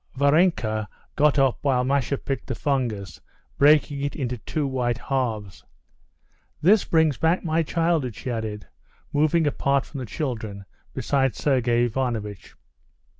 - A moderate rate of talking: No, slow, 130 wpm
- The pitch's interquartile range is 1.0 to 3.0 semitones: No, average, 3.9 semitones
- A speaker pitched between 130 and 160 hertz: Yes, low, 135 Hz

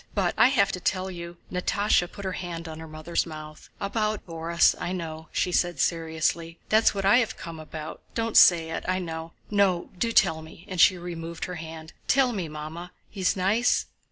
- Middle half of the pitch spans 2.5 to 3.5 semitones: Yes, average, 3.2 semitones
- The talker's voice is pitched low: No, medium, 175 Hz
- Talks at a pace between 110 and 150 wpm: No, average, 190 wpm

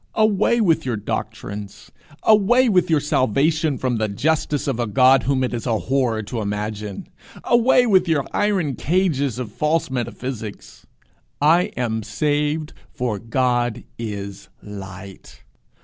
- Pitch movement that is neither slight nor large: No, wide, 6.5 semitones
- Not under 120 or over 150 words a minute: Yes, slow, 135 wpm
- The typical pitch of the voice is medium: No, low, 130 Hz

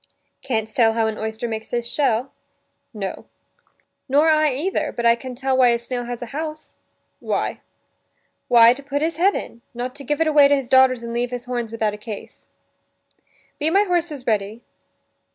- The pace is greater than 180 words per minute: Yes, average, 190 wpm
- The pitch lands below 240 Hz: No, high, 245 Hz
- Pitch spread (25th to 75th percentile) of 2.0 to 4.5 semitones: Yes, average, 3.7 semitones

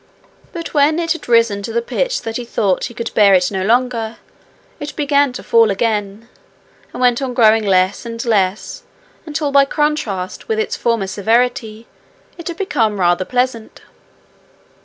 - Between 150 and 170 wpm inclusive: Yes, average, 165 wpm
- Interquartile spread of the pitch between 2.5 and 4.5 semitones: No, average, 5.2 semitones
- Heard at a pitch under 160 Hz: No, high, 230 Hz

